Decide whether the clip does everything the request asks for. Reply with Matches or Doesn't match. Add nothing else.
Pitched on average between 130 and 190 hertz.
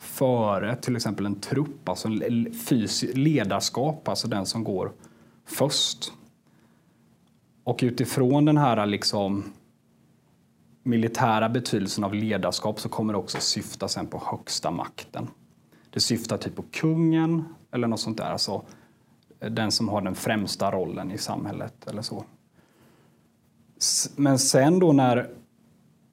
Doesn't match